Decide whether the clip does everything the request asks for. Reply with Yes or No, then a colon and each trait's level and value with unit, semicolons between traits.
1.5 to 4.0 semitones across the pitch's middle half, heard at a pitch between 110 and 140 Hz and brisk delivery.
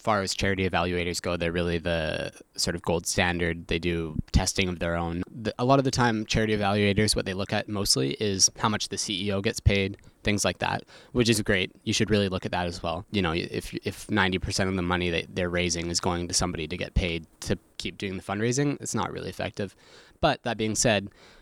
No: average, 3.5 semitones; very low, 95 Hz; fast, 235 wpm